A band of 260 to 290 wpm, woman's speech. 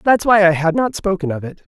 Yes: fast, 275 wpm; female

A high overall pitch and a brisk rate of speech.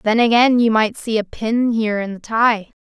Yes: high, 225 Hz; fast, 235 wpm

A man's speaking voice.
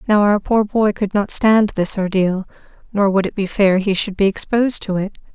No: female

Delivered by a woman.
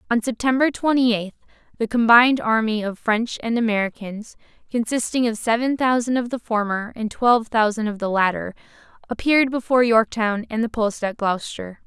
Yes: female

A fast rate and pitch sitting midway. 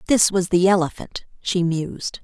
No: average, 160 wpm; medium, 180 Hz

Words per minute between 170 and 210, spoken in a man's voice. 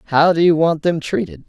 No: fast, 245 wpm; male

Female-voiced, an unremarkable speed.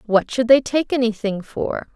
Yes: female; average, 185 wpm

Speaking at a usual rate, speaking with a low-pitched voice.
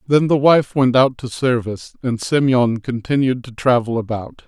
Yes: average, 175 wpm; low, 125 Hz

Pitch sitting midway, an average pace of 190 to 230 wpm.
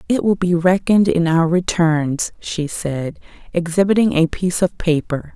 No: medium, 175 Hz; average, 155 wpm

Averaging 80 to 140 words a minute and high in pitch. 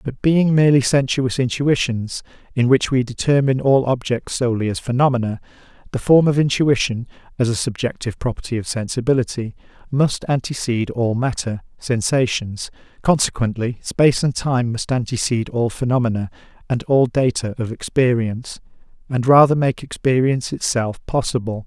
No: slow, 135 wpm; low, 125 Hz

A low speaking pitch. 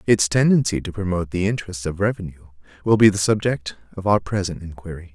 Yes: very low, 95 Hz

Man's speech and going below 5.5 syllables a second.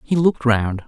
Yes: male; 5.3 syllables/s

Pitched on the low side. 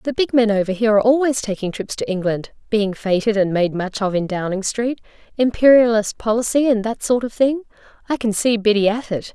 No: high, 220 Hz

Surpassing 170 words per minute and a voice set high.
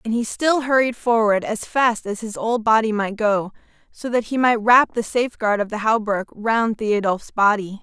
Yes: average, 200 wpm; high, 220 Hz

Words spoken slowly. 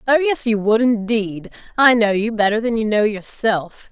No: average, 200 wpm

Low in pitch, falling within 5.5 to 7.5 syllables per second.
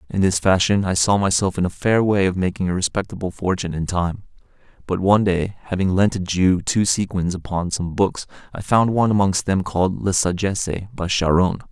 Yes: very low, 95 Hz; 5.6 syllables/s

